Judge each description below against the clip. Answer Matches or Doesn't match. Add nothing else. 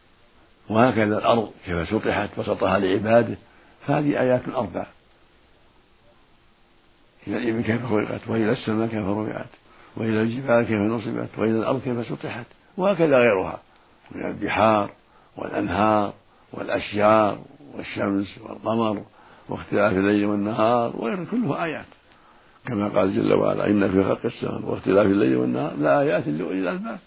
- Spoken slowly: Doesn't match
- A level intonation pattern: Matches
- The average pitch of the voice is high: Doesn't match